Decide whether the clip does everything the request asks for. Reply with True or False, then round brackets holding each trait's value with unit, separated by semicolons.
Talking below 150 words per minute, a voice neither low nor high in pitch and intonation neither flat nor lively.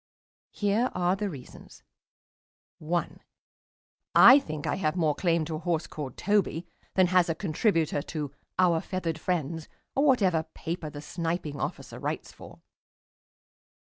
True (140 wpm; 170 Hz; 3.0 semitones)